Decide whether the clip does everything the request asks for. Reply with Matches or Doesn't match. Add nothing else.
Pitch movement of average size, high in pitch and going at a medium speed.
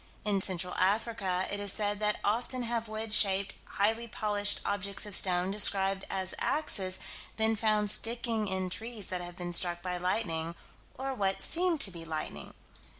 Matches